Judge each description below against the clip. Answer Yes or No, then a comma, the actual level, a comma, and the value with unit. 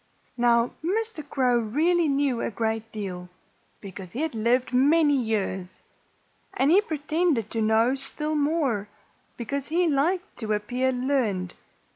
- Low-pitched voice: No, very high, 255 Hz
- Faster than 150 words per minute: No, slow, 135 wpm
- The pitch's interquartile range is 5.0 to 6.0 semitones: Yes, wide, 5.5 semitones